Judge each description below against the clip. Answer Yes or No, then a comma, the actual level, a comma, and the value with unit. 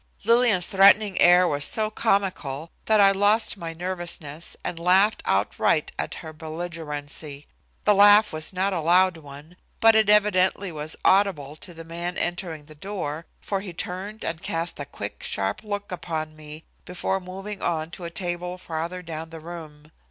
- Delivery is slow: No, average, 165 wpm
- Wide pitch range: No, average, 3.7 semitones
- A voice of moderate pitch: Yes, medium, 175 Hz